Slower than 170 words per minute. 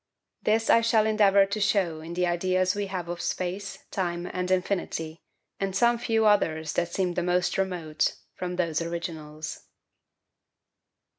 Yes: average, 150 wpm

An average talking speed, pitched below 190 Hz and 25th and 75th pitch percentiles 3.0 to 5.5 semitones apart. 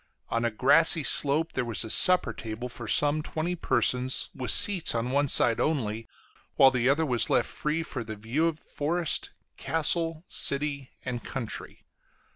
Yes: average, 165 wpm; low, 135 Hz; average, 4.8 semitones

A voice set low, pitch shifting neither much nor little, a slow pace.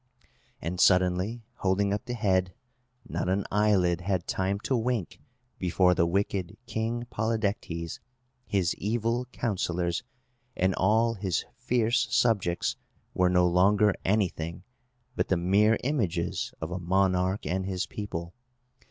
Yes: very low, 95 Hz; average, 3.2 semitones; slow, 125 wpm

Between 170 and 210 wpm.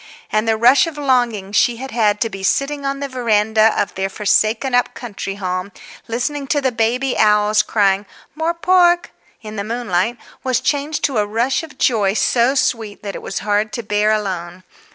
Yes: average, 190 wpm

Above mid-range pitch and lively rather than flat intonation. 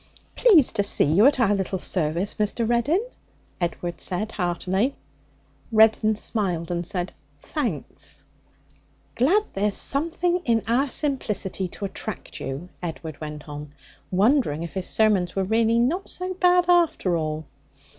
Yes: high, 205 Hz; wide, 7.1 semitones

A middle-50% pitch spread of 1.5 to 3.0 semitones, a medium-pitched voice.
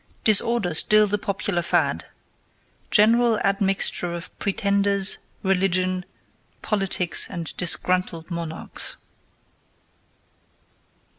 No: narrow, 2.5 semitones; high, 195 Hz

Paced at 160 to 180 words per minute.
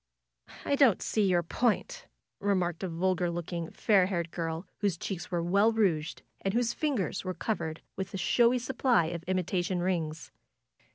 Yes: average, 165 wpm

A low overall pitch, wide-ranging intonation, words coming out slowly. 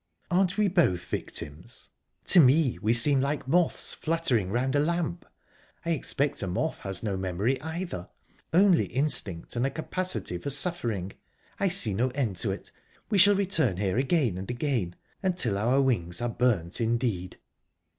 No: low, 130 Hz; wide, 8.7 semitones; average, 155 wpm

